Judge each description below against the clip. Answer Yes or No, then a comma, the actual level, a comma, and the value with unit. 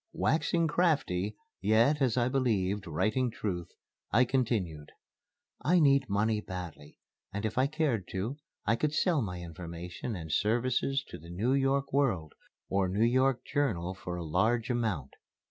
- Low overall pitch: Yes, low, 110 Hz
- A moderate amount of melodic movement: No, wide, 6.7 semitones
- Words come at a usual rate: Yes, average, 150 wpm